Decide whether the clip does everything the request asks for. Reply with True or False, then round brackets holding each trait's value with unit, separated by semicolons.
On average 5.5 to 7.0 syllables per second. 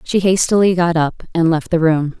False (4.9 syllables/s)